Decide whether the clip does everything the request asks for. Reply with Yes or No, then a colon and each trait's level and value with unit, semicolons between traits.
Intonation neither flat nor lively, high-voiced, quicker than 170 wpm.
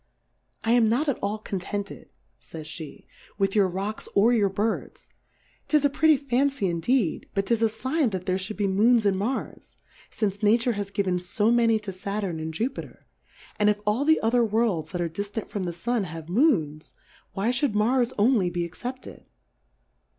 Yes: average, 4.1 semitones; high, 210 Hz; average, 180 wpm